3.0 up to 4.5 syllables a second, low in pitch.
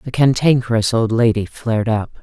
No: 5.5 syllables/s; low, 115 Hz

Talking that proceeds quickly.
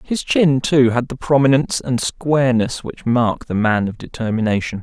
No: average, 175 wpm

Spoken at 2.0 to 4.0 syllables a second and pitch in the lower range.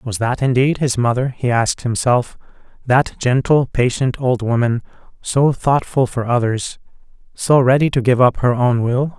No: 4.5 syllables/s; low, 125 Hz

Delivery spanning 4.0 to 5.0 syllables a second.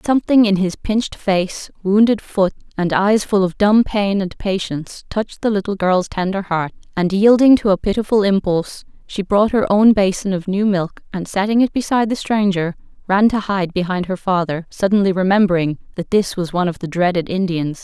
No: 5.3 syllables/s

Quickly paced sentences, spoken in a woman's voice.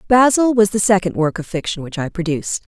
Yes: fast, 220 wpm; female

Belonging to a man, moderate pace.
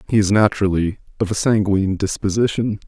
Yes: male; average, 145 wpm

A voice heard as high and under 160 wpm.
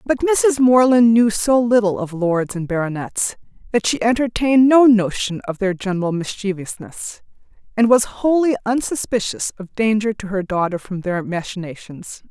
Yes: high, 215 Hz; average, 150 wpm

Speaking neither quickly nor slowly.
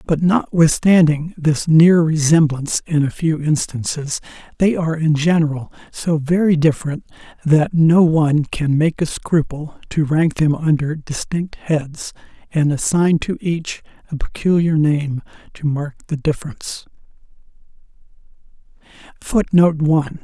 No: slow, 125 wpm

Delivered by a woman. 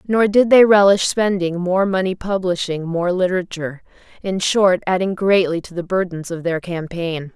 Yes: female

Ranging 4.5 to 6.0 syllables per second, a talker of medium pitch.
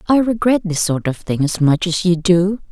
Yes: 4.9 syllables/s; medium, 180 Hz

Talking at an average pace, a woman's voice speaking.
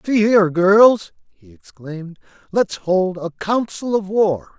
No: average, 145 wpm; male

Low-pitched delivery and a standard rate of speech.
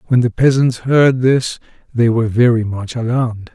Yes: low, 120 Hz; average, 170 wpm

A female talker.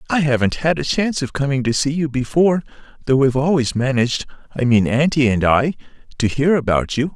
No: male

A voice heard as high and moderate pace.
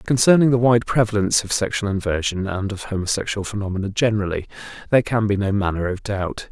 No: low, 105 Hz; average, 175 wpm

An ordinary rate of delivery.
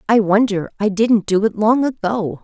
Yes: average, 195 wpm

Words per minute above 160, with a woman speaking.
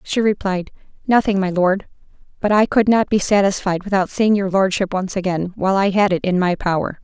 Yes: fast, 205 wpm; female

